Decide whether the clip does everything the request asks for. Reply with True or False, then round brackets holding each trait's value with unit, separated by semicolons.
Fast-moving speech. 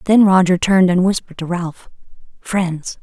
False (160 wpm)